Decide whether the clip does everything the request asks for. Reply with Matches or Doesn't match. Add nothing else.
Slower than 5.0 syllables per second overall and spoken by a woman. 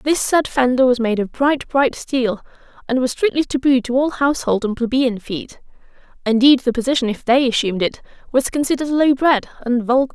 Doesn't match